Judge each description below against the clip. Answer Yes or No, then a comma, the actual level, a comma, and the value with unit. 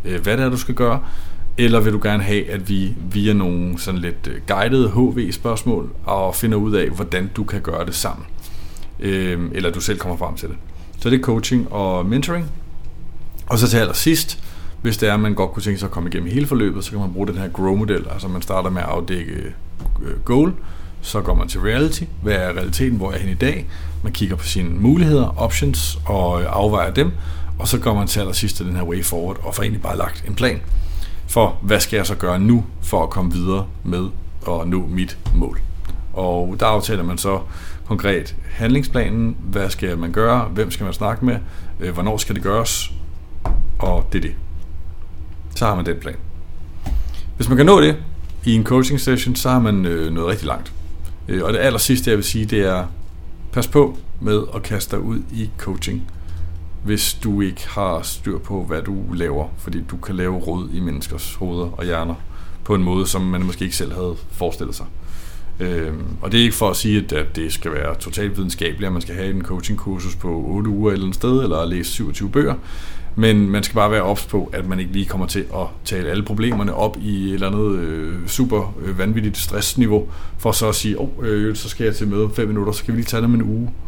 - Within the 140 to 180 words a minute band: No, average, 215 wpm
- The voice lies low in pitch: Yes, very low, 95 Hz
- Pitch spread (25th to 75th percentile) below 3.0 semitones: No, average, 4.2 semitones